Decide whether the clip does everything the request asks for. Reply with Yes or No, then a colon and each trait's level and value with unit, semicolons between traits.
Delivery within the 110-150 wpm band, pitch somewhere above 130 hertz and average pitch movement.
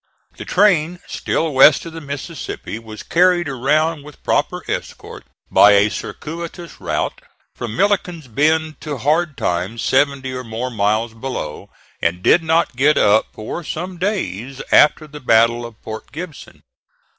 No: average, 145 wpm; medium, 140 Hz; wide, 6.1 semitones